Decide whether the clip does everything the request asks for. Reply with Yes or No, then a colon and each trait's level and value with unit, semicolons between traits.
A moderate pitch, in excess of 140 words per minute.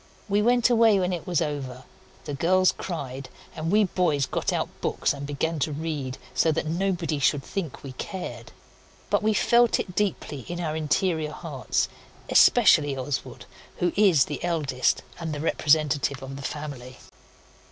Yes: medium, 155 Hz; average, 165 wpm